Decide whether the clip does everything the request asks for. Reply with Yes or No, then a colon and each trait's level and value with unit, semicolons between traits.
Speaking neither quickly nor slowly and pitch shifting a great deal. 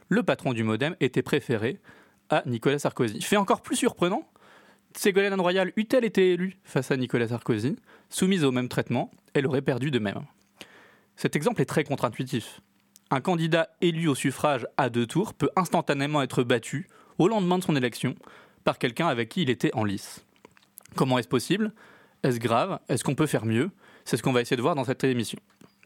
Yes: average, 190 wpm; wide, 6.0 semitones